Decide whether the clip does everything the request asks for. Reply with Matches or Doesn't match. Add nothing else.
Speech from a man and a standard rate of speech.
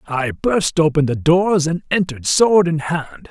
Matches